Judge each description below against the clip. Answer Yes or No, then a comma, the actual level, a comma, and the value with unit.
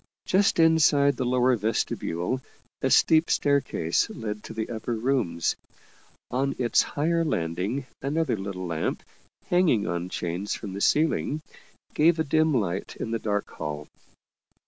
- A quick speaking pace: No, average, 140 wpm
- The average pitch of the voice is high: No, low, 120 Hz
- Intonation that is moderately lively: No, wide, 7.3 semitones